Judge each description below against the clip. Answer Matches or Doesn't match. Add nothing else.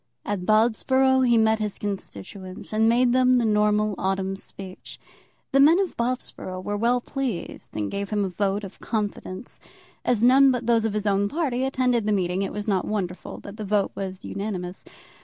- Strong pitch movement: Doesn't match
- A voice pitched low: Doesn't match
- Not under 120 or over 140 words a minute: Doesn't match